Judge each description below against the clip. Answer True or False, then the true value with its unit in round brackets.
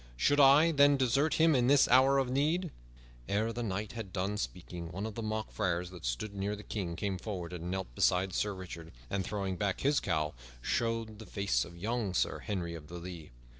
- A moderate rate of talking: False (210 wpm)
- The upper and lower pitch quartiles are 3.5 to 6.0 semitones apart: True (5.1 semitones)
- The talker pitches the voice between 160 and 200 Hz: False (100 Hz)